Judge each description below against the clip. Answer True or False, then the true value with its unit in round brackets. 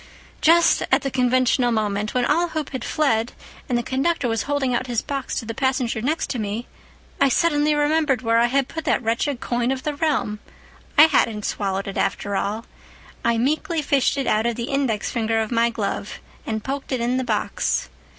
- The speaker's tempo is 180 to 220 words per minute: True (200 wpm)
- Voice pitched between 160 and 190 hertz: False (250 Hz)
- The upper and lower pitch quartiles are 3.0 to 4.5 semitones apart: True (3.8 semitones)